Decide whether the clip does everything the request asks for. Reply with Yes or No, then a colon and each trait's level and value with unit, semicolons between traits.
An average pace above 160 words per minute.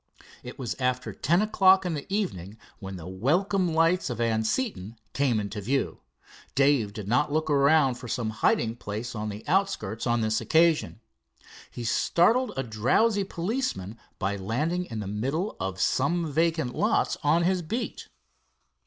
No: average, 155 wpm